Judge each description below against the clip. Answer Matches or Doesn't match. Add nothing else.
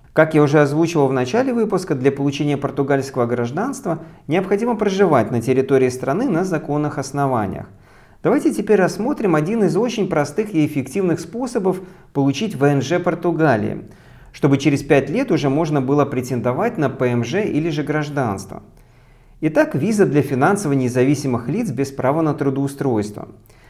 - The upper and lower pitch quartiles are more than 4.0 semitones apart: Matches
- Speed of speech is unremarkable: Matches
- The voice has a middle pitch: Matches